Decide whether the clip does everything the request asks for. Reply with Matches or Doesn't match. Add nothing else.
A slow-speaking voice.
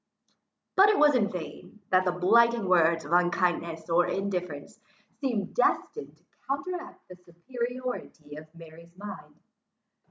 Matches